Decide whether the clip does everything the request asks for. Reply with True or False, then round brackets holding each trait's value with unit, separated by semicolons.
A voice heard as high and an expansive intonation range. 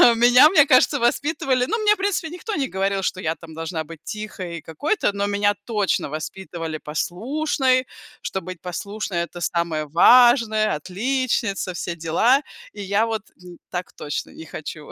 True (200 Hz; 7.1 semitones)